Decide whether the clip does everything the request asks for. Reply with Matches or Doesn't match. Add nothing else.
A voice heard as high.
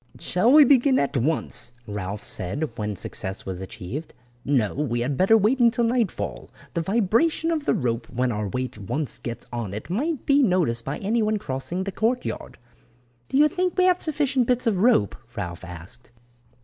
Doesn't match